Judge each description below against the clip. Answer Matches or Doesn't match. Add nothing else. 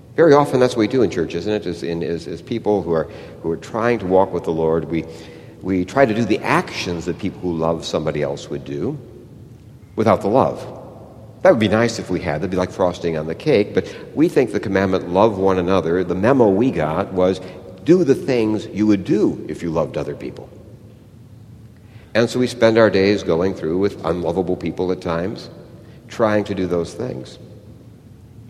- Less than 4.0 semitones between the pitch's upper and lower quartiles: Doesn't match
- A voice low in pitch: Matches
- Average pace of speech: Doesn't match